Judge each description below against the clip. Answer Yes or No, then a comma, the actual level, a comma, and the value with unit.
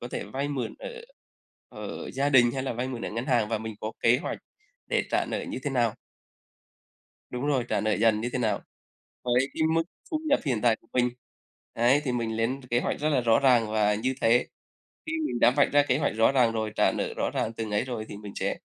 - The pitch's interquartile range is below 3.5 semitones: Yes, average, 3.0 semitones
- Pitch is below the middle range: Yes, low, 120 Hz